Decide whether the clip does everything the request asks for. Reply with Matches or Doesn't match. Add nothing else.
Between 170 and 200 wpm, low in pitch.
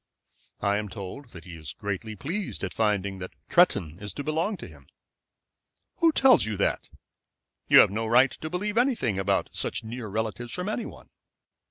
Matches